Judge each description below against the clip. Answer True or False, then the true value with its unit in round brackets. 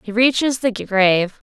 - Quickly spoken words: False (160 wpm)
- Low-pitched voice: False (220 Hz)